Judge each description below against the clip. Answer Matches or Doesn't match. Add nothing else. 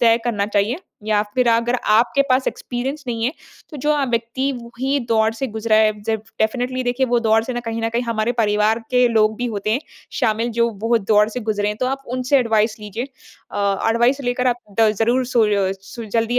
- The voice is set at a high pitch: Matches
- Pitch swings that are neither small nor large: Doesn't match